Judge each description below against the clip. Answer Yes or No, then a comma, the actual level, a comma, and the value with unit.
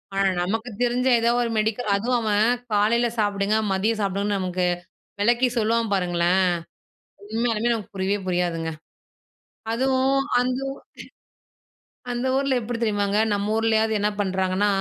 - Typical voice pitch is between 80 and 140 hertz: No, high, 215 Hz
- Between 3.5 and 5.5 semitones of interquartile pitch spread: No, average, 3.1 semitones